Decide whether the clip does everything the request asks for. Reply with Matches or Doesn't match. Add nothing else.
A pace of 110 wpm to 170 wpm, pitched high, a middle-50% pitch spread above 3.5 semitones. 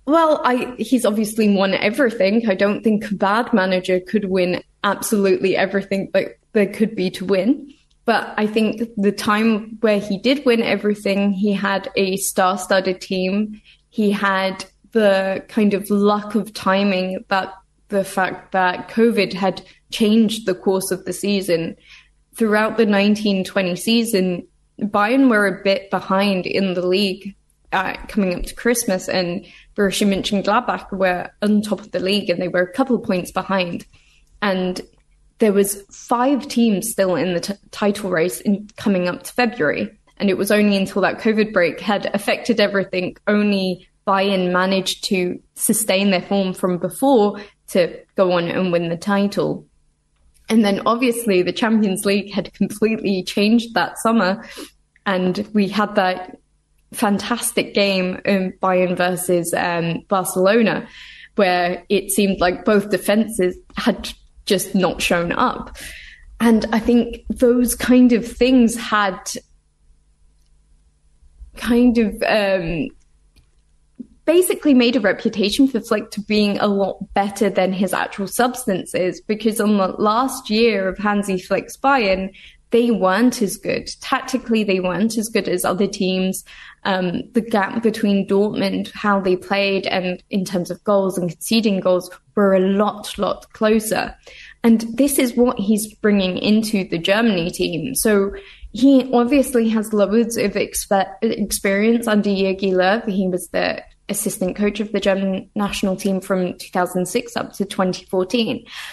Doesn't match